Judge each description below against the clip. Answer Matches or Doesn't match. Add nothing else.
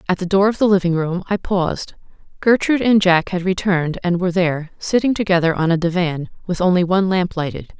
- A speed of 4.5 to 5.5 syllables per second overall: Doesn't match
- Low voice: Doesn't match